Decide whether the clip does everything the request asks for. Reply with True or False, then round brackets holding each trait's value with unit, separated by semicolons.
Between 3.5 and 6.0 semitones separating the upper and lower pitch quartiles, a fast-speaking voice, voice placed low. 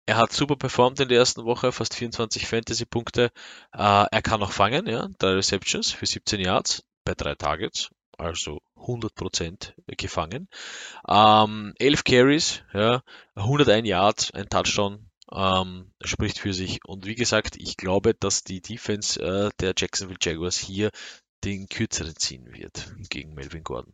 False (3.8 semitones; 150 wpm; 105 Hz)